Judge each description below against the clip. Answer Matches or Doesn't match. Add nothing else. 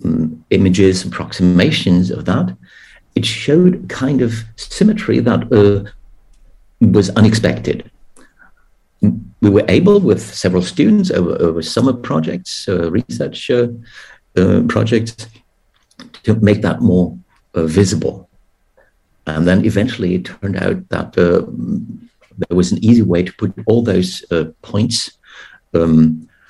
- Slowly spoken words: Matches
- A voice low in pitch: Matches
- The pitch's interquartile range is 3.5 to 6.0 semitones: Matches